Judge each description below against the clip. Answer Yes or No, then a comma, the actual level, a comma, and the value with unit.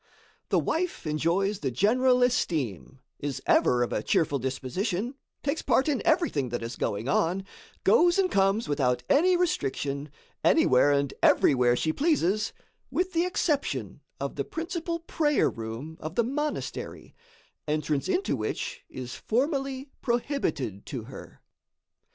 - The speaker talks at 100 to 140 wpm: Yes, slow, 135 wpm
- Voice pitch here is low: No, high, 195 Hz